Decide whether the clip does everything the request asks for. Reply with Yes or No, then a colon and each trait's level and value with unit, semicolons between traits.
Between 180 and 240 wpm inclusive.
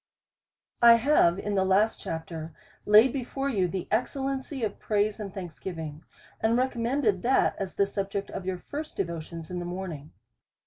No: average, 170 wpm